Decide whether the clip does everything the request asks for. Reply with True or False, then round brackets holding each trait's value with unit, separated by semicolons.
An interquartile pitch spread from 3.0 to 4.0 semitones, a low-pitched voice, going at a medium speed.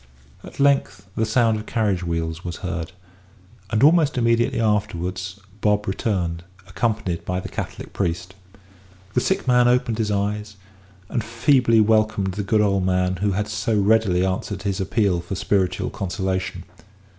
True (3.4 semitones; 100 Hz; 150 wpm)